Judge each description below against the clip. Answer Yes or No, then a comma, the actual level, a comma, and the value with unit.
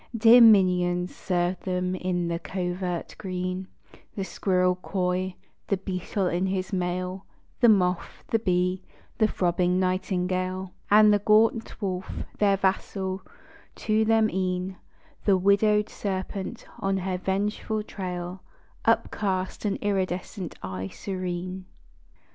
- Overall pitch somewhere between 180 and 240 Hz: Yes, medium, 185 Hz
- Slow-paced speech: Yes, slow, 120 wpm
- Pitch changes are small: Yes, narrow, 1.6 semitones